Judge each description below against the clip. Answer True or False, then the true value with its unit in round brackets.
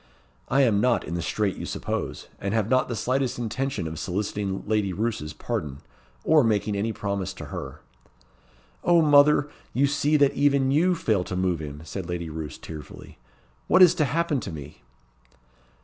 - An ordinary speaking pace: True (175 wpm)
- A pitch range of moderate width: False (7.4 semitones)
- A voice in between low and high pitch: False (110 Hz)